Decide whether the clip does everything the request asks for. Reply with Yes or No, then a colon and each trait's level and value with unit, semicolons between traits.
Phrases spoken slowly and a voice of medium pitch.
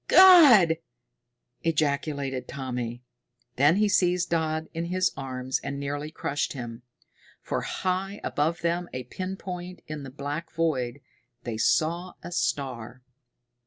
Yes: slow, 125 wpm; medium, 155 Hz